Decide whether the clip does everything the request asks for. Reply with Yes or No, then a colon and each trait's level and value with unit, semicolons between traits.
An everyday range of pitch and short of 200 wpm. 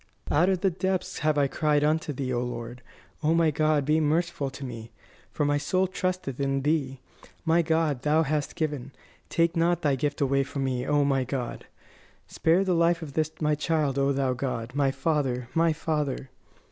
Yes: average, 3.1 semitones; average, 190 wpm